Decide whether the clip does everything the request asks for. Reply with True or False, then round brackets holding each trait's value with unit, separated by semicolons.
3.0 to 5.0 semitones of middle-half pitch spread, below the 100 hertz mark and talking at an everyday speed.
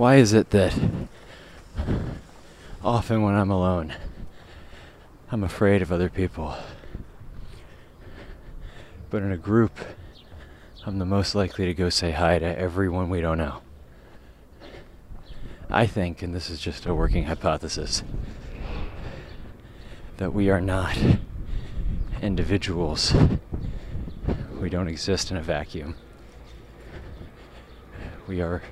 False (3.7 semitones; 90 Hz; 110 wpm)